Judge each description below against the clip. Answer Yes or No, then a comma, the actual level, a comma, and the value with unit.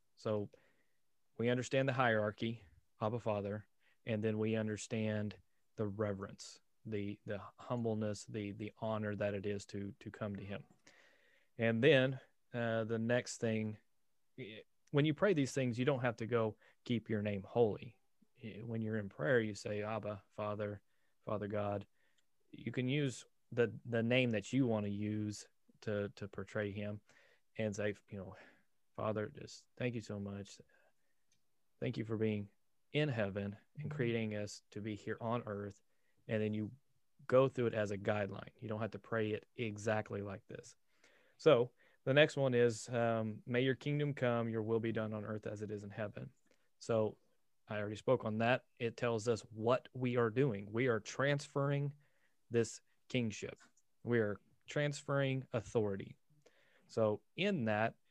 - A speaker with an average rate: Yes, average, 165 wpm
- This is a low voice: Yes, low, 110 Hz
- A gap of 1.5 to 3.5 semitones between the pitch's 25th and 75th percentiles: Yes, average, 2.7 semitones